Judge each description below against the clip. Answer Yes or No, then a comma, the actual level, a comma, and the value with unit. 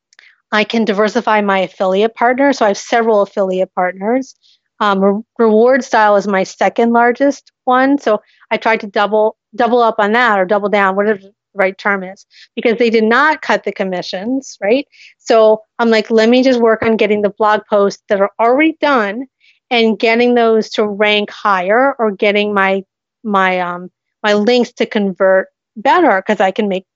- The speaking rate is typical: Yes, average, 185 wpm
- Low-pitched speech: No, high, 215 Hz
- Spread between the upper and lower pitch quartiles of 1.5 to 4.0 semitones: Yes, average, 2.9 semitones